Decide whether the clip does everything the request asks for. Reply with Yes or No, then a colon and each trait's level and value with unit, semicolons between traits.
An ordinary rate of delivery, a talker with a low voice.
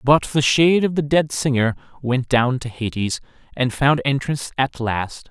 Yes: average, 180 wpm; low, 130 Hz